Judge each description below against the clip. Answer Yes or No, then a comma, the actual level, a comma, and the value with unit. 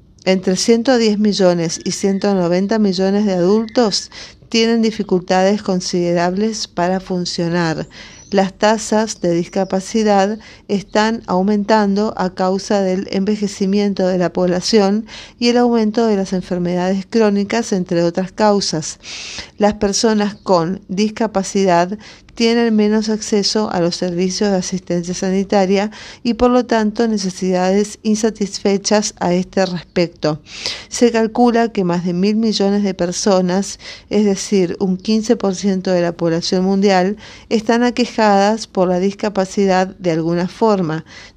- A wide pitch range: No, narrow, 2.6 semitones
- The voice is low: No, high, 195 Hz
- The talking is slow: Yes, slow, 120 wpm